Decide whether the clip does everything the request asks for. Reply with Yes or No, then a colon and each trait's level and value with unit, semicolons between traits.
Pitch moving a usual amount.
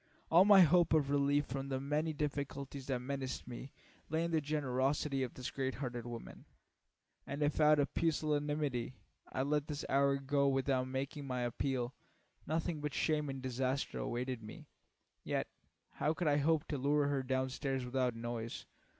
No: narrow, 2.3 semitones